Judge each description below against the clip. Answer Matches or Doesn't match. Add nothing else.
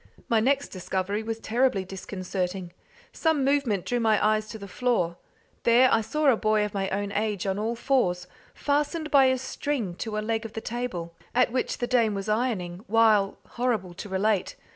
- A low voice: Doesn't match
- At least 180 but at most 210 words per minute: Matches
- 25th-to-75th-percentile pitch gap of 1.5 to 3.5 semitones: Doesn't match